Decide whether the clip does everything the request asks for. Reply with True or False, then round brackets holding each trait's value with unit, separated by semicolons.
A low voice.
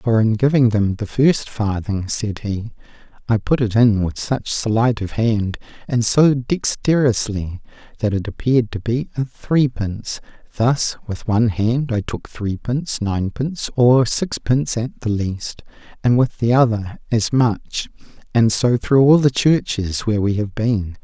True (115 Hz)